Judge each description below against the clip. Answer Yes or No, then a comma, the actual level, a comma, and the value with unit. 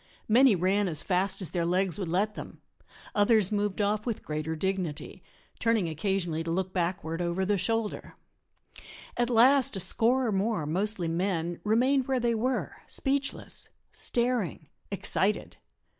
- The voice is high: Yes, high, 200 Hz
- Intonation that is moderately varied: Yes, average, 4.6 semitones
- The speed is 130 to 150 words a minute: Yes, average, 145 wpm